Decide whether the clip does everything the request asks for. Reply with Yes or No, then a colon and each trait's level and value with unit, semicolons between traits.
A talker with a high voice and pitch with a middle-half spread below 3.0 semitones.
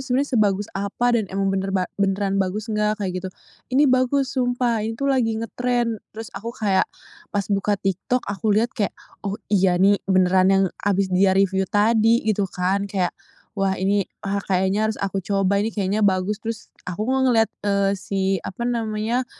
Yes: high, 205 Hz; narrow, 2.6 semitones